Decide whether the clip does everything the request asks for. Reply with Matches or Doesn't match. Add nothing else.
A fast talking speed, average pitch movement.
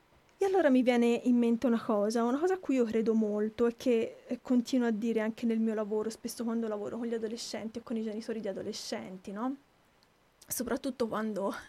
Doesn't match